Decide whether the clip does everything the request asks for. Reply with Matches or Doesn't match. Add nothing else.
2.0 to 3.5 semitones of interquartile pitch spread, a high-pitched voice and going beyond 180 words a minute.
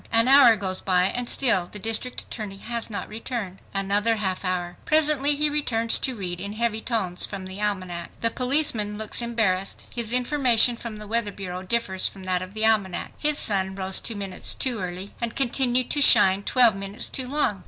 Doesn't match